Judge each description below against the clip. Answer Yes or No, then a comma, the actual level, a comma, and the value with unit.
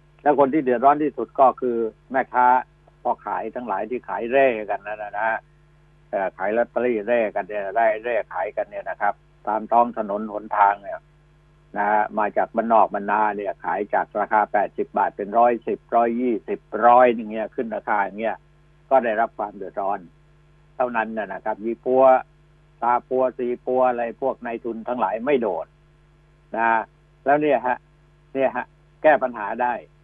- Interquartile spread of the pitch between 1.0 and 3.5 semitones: No, average, 4.6 semitones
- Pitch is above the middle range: No, low, 125 Hz